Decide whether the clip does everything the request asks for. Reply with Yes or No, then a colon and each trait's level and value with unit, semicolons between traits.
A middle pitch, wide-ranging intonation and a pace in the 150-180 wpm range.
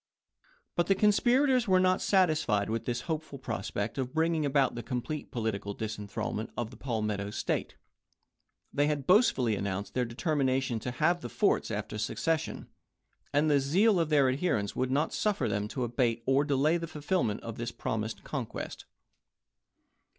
No: low, 130 Hz; wide, 6.0 semitones; average, 160 wpm